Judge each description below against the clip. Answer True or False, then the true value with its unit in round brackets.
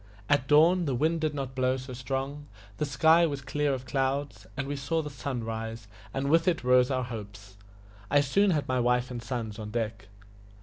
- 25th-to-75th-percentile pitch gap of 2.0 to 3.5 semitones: True (3.2 semitones)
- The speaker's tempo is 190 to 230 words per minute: True (205 wpm)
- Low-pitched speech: True (130 Hz)